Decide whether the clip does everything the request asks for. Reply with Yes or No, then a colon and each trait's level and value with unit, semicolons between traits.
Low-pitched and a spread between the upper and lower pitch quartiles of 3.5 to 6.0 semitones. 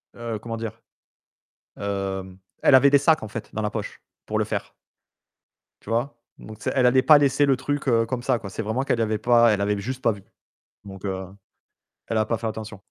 Yes: low, 115 Hz; average, 3.8 semitones